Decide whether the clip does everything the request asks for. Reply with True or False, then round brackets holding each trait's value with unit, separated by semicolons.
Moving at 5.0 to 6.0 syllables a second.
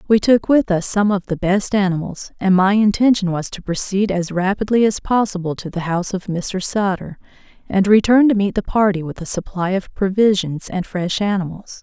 True (5.2 syllables/s)